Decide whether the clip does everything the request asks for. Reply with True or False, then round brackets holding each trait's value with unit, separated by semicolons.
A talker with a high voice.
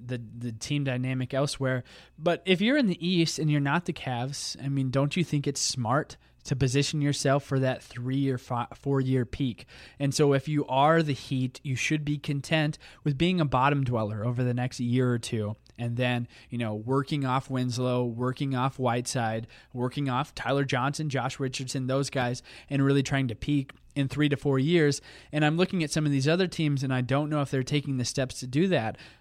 False (135 Hz)